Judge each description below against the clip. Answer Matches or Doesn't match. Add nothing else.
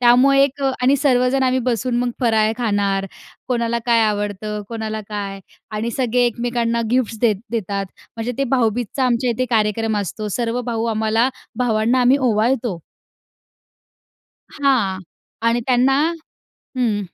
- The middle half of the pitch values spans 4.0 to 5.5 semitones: Doesn't match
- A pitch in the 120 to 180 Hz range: Doesn't match